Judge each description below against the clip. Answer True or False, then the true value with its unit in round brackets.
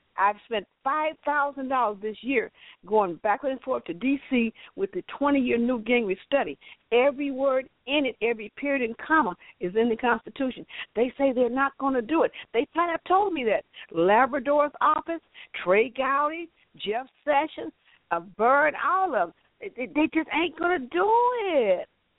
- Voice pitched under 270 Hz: False (275 Hz)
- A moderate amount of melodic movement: True (4.9 semitones)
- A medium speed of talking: True (170 wpm)